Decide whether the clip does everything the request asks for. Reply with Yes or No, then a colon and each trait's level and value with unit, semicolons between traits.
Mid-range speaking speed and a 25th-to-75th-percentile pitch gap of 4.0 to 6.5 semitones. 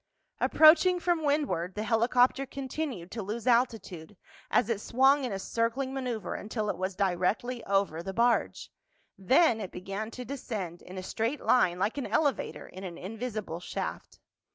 Yes: average, 160 wpm; average, 5.2 semitones